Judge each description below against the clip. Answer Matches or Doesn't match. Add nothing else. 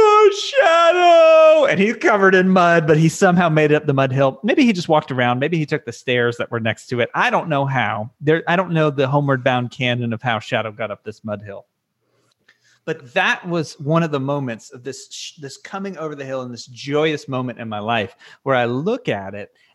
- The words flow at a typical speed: Doesn't match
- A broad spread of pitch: Matches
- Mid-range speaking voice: Matches